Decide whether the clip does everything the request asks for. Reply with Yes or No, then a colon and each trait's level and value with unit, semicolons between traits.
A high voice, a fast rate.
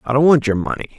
No: low, 125 Hz; fast, 305 wpm